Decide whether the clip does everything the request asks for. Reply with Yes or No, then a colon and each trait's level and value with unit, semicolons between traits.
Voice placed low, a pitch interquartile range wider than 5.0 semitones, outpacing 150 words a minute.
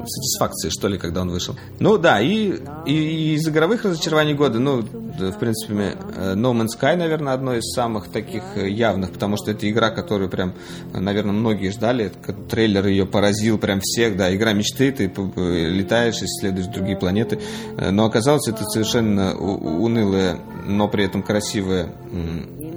No: low, 105 Hz; average, 3.7 semitones; fast, 160 wpm